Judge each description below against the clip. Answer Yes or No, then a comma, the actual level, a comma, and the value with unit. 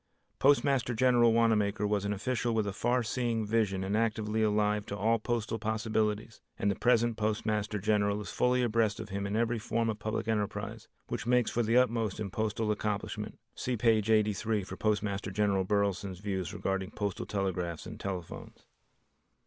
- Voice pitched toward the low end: Yes, low, 105 Hz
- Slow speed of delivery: No, average, 170 wpm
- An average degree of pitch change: No, narrow, 2.0 semitones